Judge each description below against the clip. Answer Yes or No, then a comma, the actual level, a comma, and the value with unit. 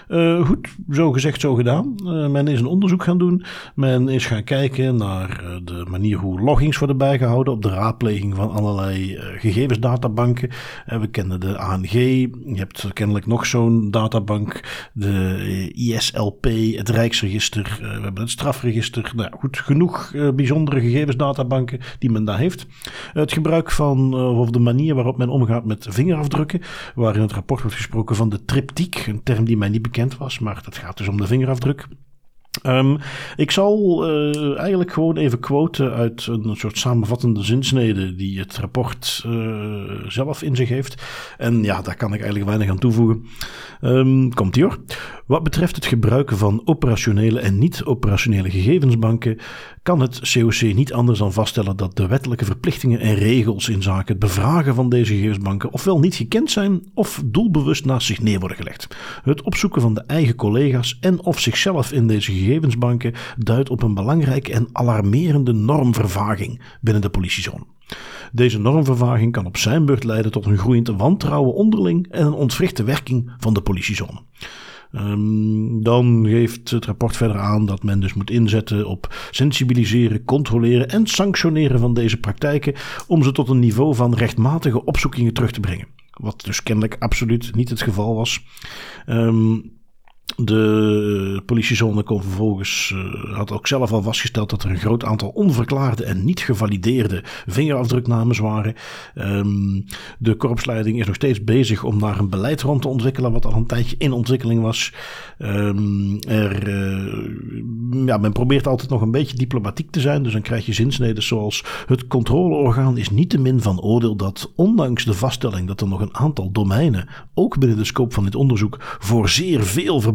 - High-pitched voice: No, low, 120 Hz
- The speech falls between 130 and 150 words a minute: No, average, 170 wpm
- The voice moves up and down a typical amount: Yes, average, 4.0 semitones